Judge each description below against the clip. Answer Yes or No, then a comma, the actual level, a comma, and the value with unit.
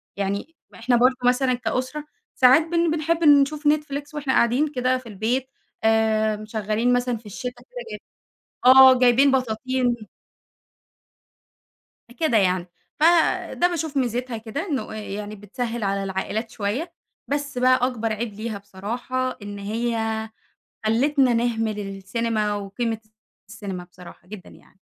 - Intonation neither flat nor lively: Yes, average, 3.7 semitones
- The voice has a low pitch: No, high, 240 Hz